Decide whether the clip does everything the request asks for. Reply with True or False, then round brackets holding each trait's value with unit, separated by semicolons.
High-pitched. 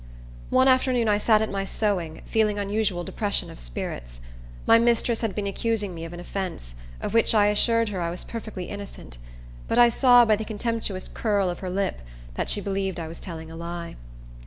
True (205 Hz)